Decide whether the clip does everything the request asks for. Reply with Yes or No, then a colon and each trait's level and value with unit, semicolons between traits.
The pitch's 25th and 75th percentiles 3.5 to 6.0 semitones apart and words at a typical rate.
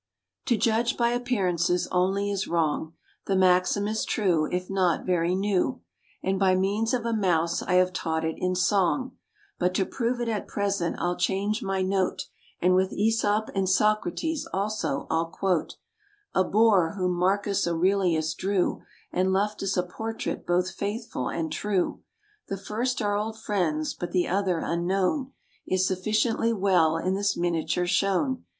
No: average, 2.8 semitones; average, 160 wpm